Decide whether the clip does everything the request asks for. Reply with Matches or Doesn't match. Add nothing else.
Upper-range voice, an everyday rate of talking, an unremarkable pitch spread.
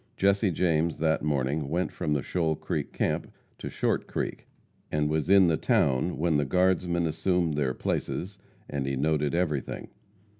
Doesn't match